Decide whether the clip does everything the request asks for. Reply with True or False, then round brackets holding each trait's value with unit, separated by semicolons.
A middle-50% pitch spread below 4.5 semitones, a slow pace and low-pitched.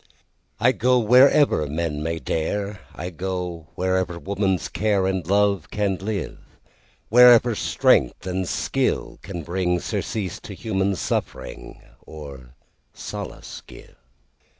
True (3.3 semitones; 95 wpm; 95 Hz)